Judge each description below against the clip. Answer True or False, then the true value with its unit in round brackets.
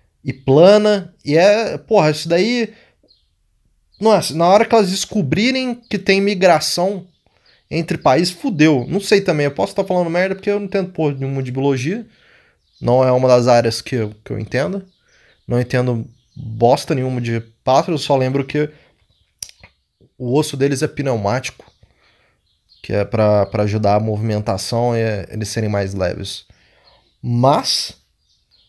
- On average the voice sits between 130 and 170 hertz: True (135 Hz)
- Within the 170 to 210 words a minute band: False (155 wpm)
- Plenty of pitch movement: True (8.8 semitones)